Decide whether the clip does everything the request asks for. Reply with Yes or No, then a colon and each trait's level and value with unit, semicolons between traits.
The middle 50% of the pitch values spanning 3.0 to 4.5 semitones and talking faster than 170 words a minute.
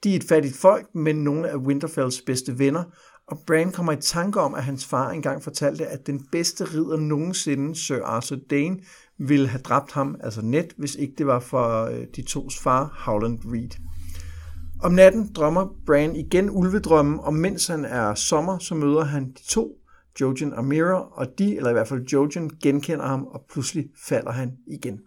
Yes: average, 3.7 semitones; average, 190 wpm